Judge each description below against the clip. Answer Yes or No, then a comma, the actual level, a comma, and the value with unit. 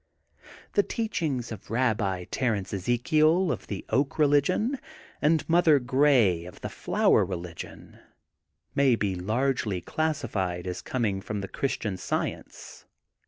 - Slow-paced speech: Yes, slow, 115 wpm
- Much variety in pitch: Yes, wide, 7.4 semitones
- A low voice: Yes, low, 120 Hz